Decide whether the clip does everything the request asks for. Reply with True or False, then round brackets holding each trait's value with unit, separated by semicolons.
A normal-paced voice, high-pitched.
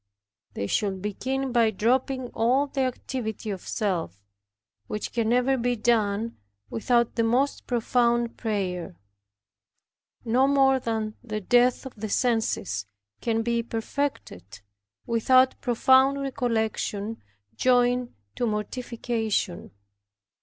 False (110 wpm; 235 Hz)